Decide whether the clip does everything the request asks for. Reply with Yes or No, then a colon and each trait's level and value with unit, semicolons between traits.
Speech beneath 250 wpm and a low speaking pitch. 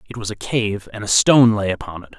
No: fast, 275 wpm; low, 105 Hz